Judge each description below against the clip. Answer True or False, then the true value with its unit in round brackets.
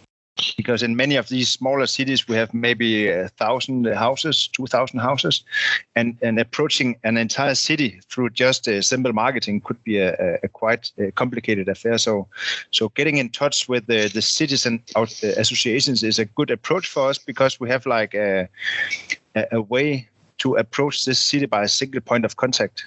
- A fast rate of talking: False (175 wpm)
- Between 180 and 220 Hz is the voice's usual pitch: False (120 Hz)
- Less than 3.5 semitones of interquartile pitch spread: True (3.0 semitones)